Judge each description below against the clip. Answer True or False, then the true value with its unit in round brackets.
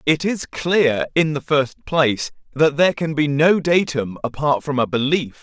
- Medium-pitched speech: True (150 Hz)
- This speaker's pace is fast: False (190 wpm)